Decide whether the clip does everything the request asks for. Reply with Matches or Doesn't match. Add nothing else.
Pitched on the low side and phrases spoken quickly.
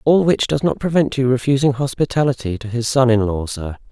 Matches